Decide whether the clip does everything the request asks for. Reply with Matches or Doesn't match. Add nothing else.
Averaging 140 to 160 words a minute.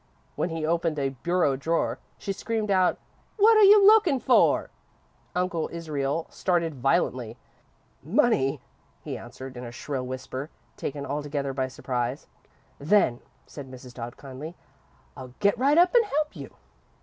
Matches